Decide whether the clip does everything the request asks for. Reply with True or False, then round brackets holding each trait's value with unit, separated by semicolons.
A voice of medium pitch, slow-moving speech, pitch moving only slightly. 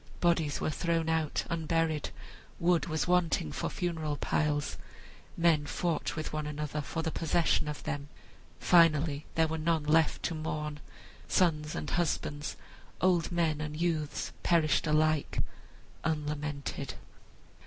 True (155 Hz; 130 wpm; 1.8 semitones)